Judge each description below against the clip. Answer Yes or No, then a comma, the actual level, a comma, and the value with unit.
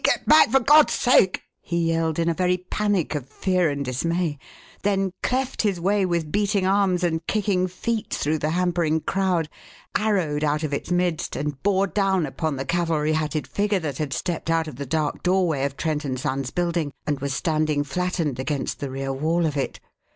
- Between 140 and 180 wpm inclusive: No, average, 195 wpm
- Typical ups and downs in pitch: Yes, average, 4.0 semitones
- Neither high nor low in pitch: Yes, medium, 165 Hz